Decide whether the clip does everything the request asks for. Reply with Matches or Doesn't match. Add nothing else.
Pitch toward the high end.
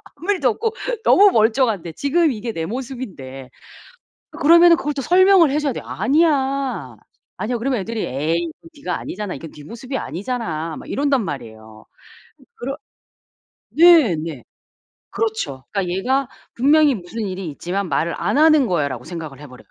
Matches